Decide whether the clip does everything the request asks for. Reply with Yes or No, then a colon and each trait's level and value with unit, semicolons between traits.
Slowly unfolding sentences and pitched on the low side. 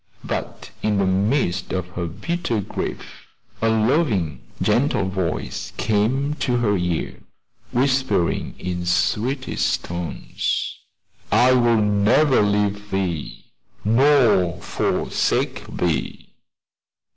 Yes: slow, 100 wpm; low, 105 Hz